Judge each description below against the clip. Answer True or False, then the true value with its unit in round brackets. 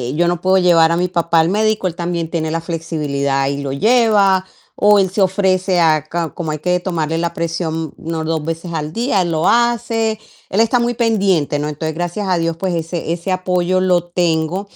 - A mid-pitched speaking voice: True (175 Hz)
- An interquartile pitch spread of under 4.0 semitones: True (2.8 semitones)